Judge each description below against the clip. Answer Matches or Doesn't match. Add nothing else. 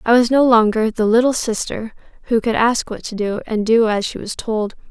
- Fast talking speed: Matches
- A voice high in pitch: Matches